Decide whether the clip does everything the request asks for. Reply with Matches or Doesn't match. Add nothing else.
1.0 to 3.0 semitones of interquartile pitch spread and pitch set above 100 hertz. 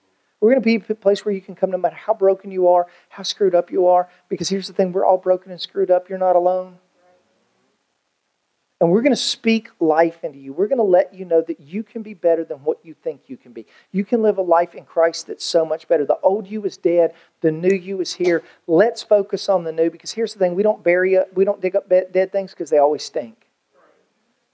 Matches